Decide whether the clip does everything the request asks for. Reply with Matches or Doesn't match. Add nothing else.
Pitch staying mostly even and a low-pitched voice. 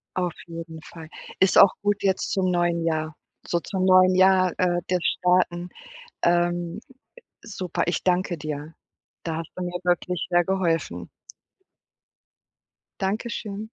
Doesn't match